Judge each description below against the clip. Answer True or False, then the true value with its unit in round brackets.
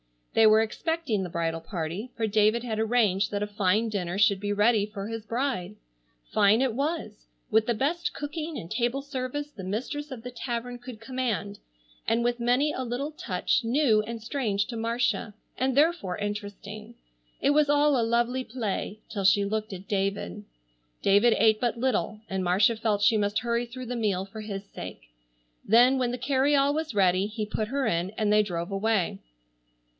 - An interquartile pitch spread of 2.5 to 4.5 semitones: True (3.7 semitones)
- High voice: True (225 Hz)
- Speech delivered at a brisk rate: False (185 wpm)